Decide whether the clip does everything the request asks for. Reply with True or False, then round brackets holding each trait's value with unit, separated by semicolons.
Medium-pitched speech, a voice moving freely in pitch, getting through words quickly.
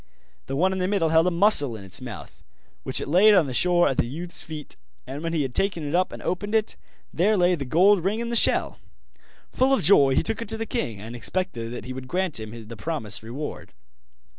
True (165 Hz; 6.8 semitones; 240 wpm)